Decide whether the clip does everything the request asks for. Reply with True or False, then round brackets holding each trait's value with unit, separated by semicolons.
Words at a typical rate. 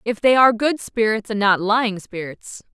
True (195 wpm)